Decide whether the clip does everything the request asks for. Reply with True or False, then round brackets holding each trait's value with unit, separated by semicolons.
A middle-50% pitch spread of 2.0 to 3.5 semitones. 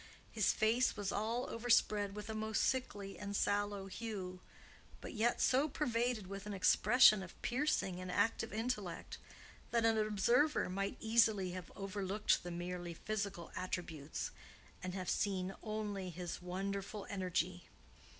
True (3.2 semitones)